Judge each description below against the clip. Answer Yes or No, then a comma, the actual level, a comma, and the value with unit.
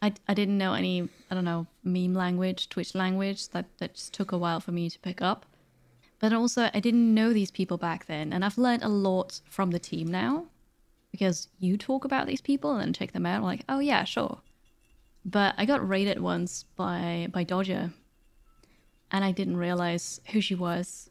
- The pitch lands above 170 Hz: Yes, medium, 185 Hz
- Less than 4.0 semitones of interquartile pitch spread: Yes, average, 3.2 semitones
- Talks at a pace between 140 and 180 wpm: No, fast, 205 wpm